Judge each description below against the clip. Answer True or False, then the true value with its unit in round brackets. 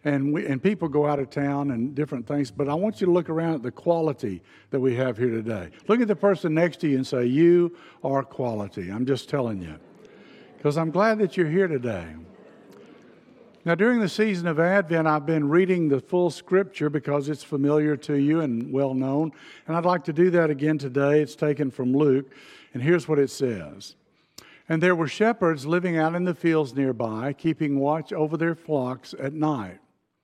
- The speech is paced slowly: False (205 wpm)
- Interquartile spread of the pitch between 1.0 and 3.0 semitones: False (3.9 semitones)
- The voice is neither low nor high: True (150 Hz)